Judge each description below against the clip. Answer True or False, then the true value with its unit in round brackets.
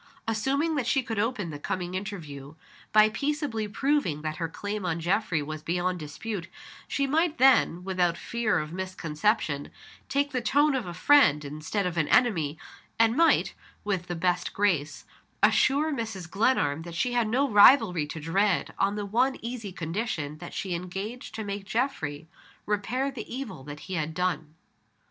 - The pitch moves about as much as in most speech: False (6.4 semitones)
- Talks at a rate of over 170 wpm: False (165 wpm)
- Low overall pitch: False (200 Hz)